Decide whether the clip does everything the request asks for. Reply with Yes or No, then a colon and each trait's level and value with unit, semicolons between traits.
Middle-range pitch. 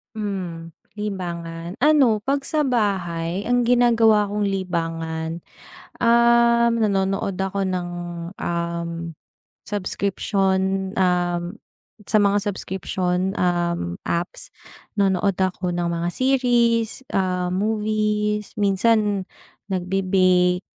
No: high, 195 Hz